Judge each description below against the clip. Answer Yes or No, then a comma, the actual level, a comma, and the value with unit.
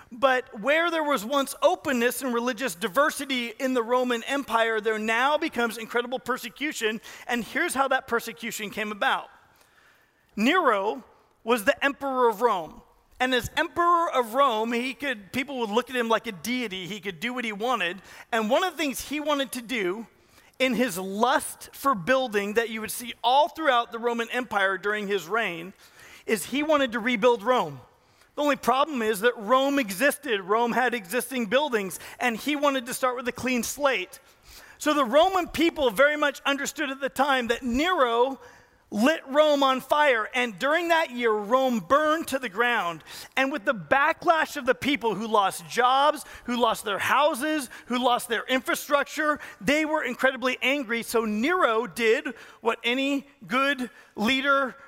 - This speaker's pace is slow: No, average, 175 wpm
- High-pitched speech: Yes, very high, 255 Hz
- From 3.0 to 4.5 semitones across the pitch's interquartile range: Yes, average, 3.4 semitones